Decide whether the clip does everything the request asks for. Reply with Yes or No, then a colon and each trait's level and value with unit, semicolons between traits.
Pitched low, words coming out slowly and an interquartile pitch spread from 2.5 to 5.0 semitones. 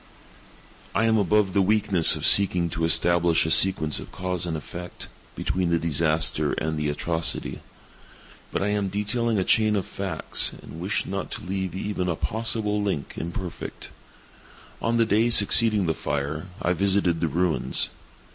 No: very low, 90 Hz; average, 155 wpm; average, 3.8 semitones